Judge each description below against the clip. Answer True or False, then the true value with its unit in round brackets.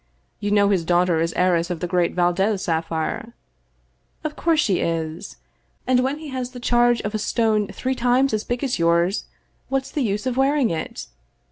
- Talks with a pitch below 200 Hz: False (210 Hz)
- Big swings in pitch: True (6.4 semitones)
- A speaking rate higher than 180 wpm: True (200 wpm)